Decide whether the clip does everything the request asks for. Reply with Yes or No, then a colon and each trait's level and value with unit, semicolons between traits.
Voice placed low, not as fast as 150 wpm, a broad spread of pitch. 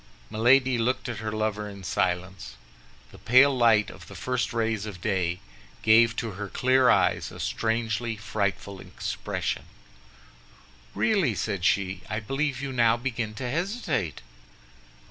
No: low, 110 Hz; average, 140 wpm; average, 3.7 semitones